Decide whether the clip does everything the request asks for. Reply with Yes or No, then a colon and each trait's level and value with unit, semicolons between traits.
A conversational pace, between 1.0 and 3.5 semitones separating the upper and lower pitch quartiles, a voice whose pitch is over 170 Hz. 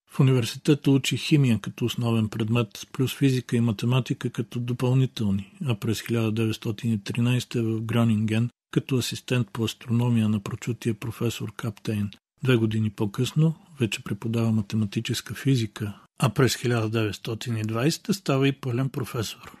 No: average, 125 wpm; narrow, 2.6 semitones; low, 120 Hz